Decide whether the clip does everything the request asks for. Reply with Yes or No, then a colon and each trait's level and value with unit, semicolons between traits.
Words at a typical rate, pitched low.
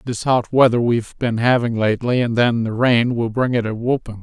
No: fast, 225 wpm; low, 120 Hz